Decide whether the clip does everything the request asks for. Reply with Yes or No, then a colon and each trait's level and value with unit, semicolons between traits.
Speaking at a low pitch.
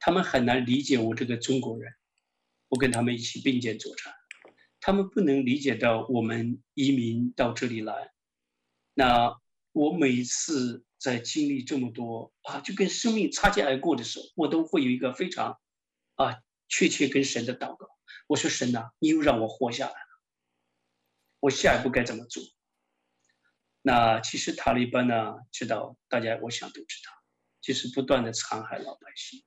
Yes: low, 120 Hz